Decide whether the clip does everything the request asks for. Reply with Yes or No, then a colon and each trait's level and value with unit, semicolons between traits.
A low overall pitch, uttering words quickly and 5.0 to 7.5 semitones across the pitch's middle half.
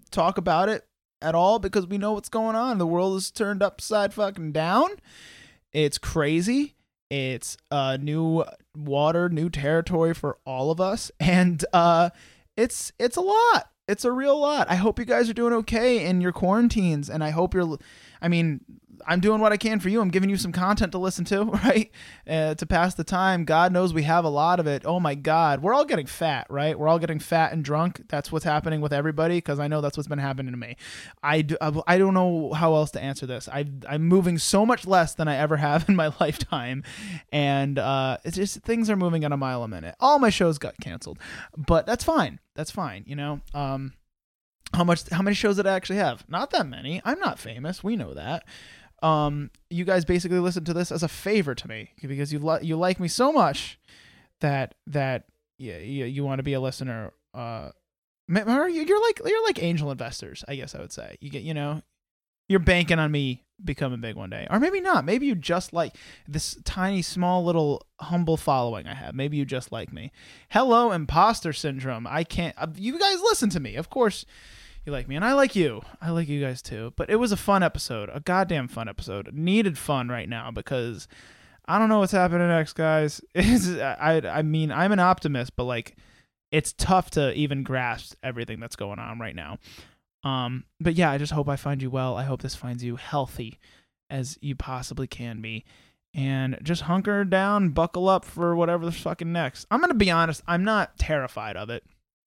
No: medium, 160 Hz; fast, 210 wpm; average, 5.3 semitones